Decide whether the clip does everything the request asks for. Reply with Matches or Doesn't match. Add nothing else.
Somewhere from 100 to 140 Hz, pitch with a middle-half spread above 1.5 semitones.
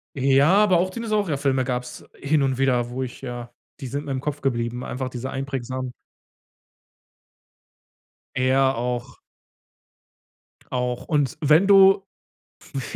Matches